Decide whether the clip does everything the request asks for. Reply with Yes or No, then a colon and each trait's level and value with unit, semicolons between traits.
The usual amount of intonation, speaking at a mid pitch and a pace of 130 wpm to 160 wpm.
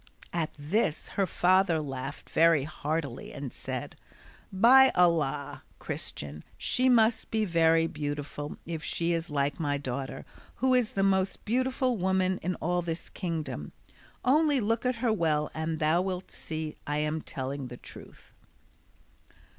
Yes: average, 4.9 semitones; medium, 165 Hz; average, 145 wpm